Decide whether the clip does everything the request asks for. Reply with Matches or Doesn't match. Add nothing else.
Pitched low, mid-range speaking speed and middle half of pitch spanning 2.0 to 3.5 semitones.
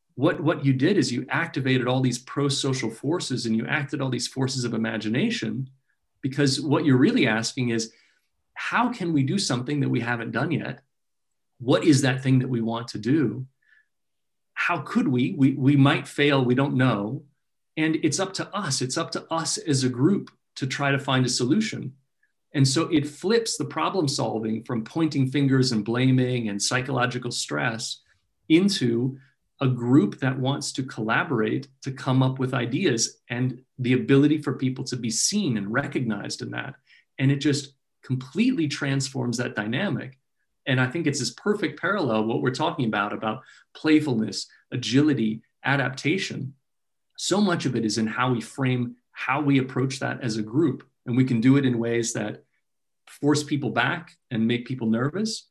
Matches